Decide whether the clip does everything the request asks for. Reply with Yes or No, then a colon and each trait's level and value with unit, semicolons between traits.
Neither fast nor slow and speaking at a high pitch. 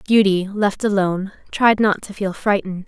Yes: average, 165 wpm; high, 200 Hz